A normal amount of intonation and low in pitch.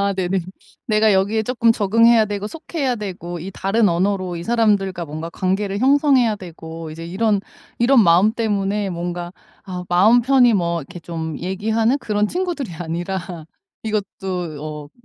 No: average, 4.3 semitones; high, 195 Hz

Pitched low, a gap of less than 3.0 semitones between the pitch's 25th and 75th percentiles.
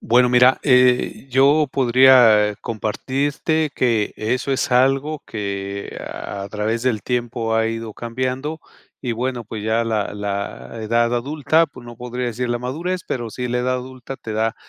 Yes: low, 120 Hz; narrow, 2.6 semitones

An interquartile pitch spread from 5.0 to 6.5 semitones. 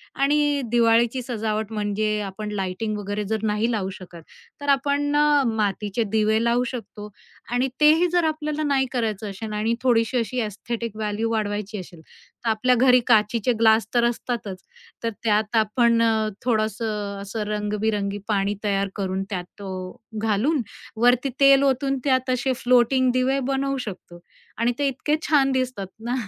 No: average, 3.6 semitones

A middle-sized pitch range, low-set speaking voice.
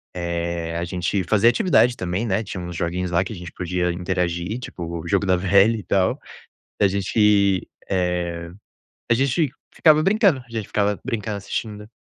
Yes: average, 3.8 semitones; very low, 95 Hz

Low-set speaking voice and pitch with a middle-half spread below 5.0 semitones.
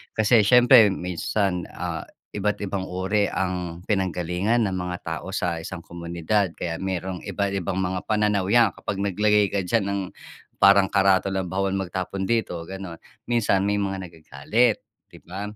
Yes: very low, 95 Hz; narrow, 2.4 semitones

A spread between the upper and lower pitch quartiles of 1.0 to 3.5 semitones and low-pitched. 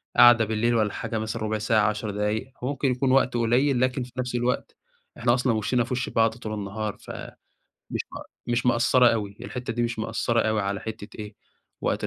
Yes: narrow, 2.4 semitones; low, 115 Hz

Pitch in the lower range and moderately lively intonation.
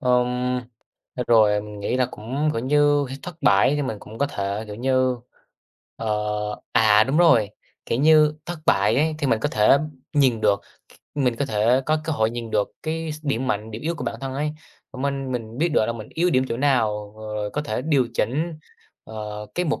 Yes: low, 125 Hz; average, 5.0 semitones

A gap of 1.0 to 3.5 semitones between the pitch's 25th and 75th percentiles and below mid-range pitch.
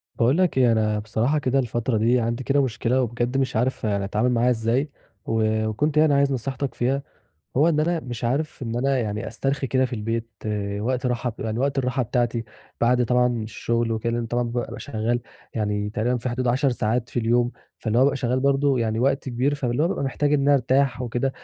Yes: average, 2.9 semitones; low, 125 Hz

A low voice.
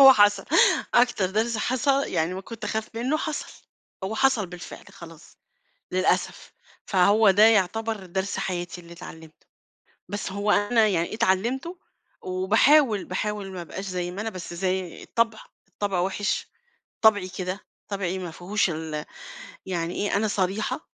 No: high, 195 Hz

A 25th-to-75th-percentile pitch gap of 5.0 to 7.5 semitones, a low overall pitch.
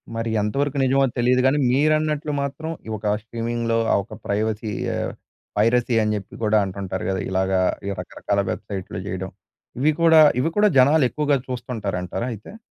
Yes: wide, 5.5 semitones; low, 120 Hz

